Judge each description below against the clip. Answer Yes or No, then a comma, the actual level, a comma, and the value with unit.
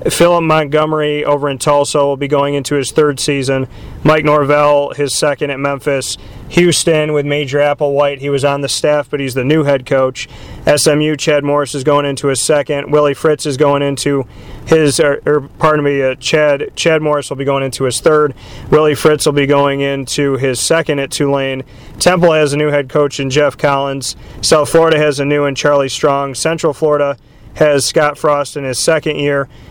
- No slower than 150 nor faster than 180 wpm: No, average, 195 wpm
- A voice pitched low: No, medium, 145 Hz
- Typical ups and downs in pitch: No, narrow, 1.4 semitones